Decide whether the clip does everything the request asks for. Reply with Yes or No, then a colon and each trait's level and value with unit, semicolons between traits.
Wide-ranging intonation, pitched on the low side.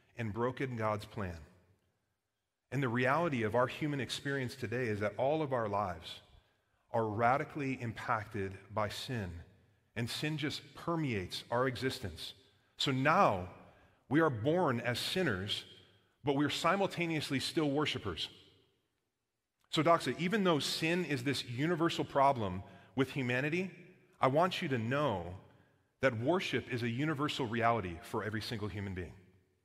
Yes: wide, 5.8 semitones; low, 125 Hz